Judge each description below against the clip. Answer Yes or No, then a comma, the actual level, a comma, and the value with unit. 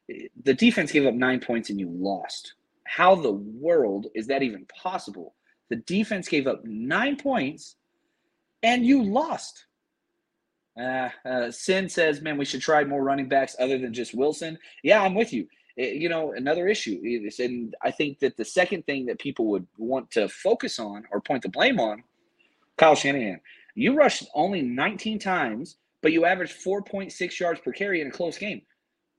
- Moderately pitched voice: Yes, medium, 165 Hz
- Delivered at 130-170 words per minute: No, average, 180 wpm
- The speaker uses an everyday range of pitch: No, wide, 9.0 semitones